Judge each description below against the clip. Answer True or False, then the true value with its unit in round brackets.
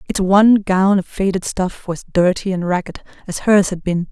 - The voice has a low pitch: False (190 Hz)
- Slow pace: False (205 wpm)